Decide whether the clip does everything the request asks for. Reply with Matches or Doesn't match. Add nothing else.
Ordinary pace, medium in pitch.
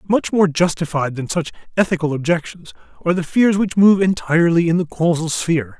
Matches